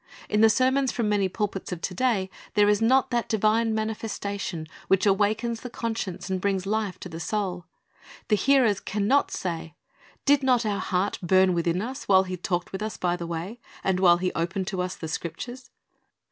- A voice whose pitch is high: Yes, high, 200 Hz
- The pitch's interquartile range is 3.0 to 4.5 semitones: Yes, average, 3.6 semitones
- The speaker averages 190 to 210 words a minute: Yes, average, 195 wpm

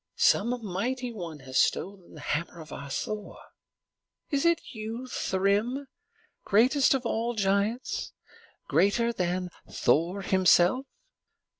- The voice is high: Yes, high, 205 Hz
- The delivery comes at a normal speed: No, slow, 115 wpm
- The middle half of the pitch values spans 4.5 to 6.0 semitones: Yes, average, 5.3 semitones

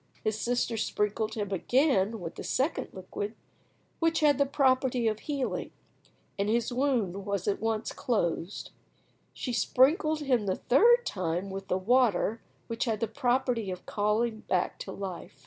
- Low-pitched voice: No, high, 225 Hz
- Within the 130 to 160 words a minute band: Yes, average, 150 wpm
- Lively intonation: No, average, 4.4 semitones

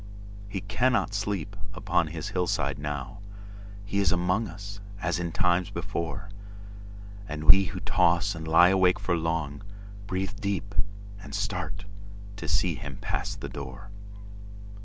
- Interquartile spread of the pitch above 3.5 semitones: No, narrow, 2.5 semitones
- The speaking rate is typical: No, slow, 120 wpm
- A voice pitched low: Yes, low, 100 Hz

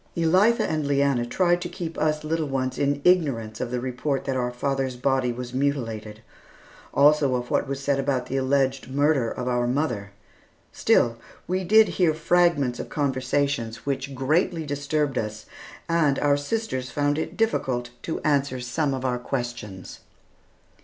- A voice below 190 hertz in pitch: Yes, medium, 140 Hz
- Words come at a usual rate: Yes, average, 160 wpm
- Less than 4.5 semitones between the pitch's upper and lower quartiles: Yes, average, 3.5 semitones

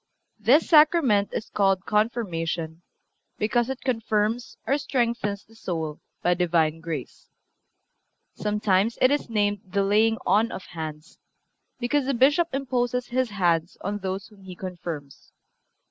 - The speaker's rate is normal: No, slow, 130 wpm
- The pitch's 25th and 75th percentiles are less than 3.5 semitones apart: No, average, 5.2 semitones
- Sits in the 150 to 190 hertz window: No, high, 210 Hz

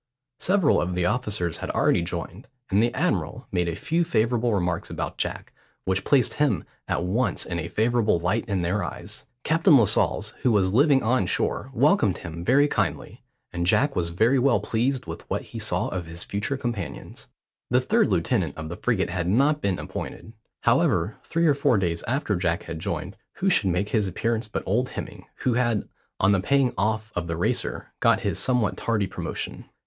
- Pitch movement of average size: No, wide, 6.0 semitones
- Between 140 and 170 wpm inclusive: No, average, 190 wpm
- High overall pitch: No, low, 105 Hz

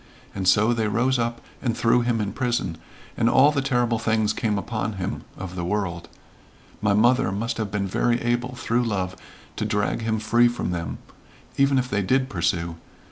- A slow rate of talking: No, average, 190 wpm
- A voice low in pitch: Yes, low, 110 Hz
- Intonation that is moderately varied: Yes, average, 3.4 semitones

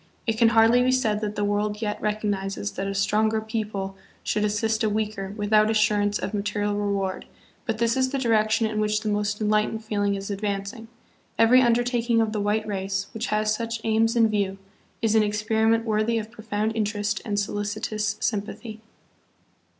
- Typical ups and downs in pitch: No, narrow, 1.4 semitones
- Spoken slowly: No, average, 180 wpm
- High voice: Yes, high, 215 Hz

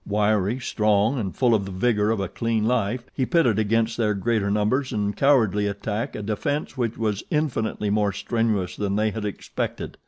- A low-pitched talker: Yes, low, 110 Hz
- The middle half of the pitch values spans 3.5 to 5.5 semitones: No, narrow, 2.4 semitones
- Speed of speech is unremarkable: Yes, average, 185 wpm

